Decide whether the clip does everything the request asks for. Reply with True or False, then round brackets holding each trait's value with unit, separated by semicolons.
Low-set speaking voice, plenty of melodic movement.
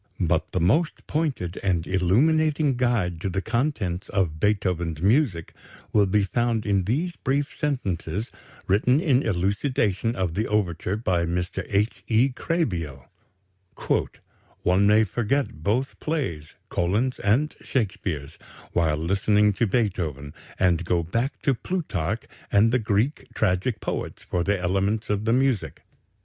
True (105 Hz; 5.8 semitones)